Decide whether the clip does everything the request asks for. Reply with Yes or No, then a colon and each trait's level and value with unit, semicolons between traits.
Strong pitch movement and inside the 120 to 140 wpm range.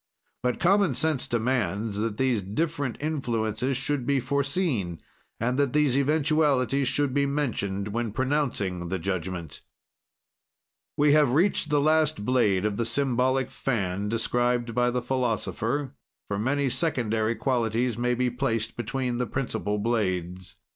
No: average, 4.4 semitones; slow, 135 wpm